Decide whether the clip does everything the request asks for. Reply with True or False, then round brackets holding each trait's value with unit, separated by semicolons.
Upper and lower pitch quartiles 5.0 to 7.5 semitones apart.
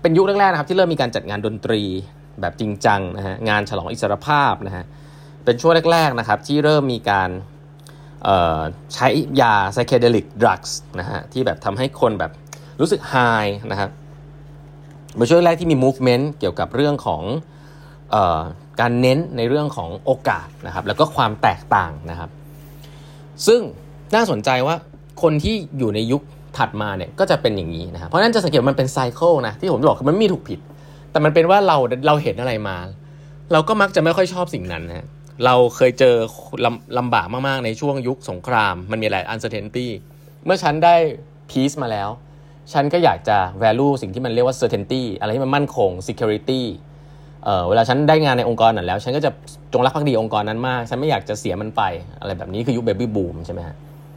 True (5.3 semitones)